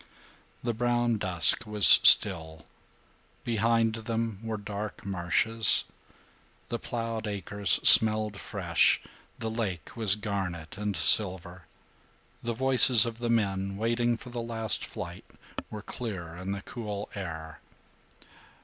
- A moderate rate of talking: No, slow, 120 wpm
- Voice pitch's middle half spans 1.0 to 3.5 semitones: Yes, average, 3.1 semitones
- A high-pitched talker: No, low, 105 Hz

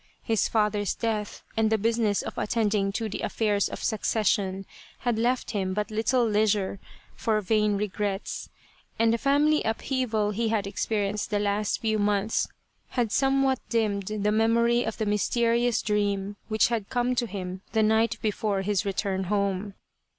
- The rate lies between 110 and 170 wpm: Yes, average, 160 wpm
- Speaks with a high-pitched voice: Yes, high, 215 Hz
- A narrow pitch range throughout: Yes, narrow, 2.0 semitones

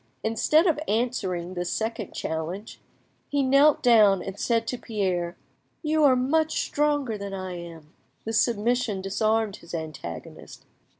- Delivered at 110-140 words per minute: Yes, slow, 135 wpm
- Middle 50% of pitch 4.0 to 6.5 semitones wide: Yes, wide, 5.4 semitones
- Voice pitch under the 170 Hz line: No, high, 220 Hz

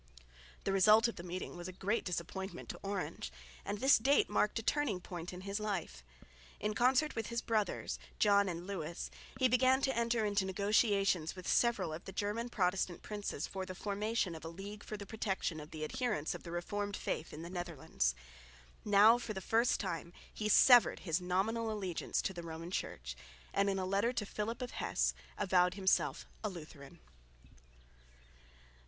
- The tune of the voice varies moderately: Yes, average, 3.7 semitones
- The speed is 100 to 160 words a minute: No, average, 180 wpm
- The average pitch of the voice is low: No, high, 195 Hz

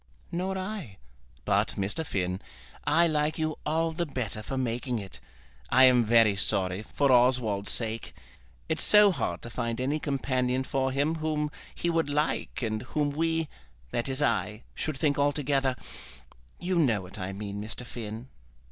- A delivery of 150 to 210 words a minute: Yes, average, 160 wpm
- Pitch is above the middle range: No, low, 130 Hz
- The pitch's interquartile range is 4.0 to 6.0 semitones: Yes, wide, 5.5 semitones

